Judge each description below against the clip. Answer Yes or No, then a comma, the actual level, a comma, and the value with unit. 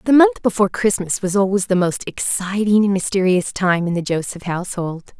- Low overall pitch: No, high, 190 Hz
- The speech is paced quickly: No, average, 185 wpm